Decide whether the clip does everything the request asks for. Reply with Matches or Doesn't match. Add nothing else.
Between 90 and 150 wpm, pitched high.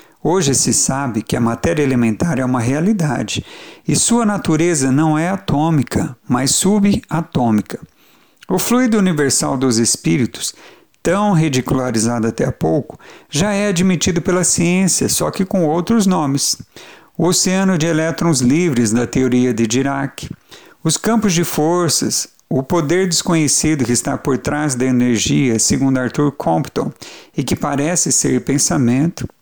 Doesn't match